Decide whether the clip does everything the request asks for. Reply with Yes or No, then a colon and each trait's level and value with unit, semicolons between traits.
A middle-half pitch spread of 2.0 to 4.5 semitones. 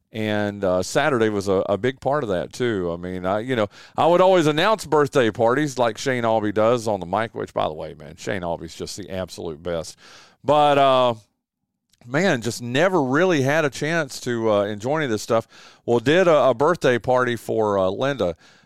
No: average, 5.2 semitones